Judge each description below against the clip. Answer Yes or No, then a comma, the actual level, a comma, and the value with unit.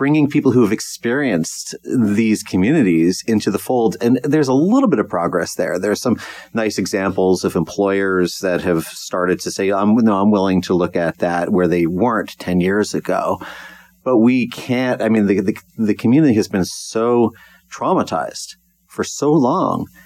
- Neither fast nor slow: Yes, average, 180 wpm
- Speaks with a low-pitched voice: Yes, low, 105 Hz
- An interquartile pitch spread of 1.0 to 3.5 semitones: No, average, 4.6 semitones